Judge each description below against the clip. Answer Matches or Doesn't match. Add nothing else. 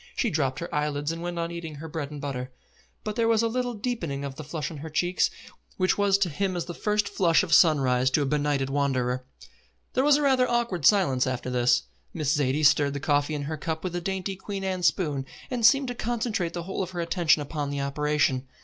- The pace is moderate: Doesn't match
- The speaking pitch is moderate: Matches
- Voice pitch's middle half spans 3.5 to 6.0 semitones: Matches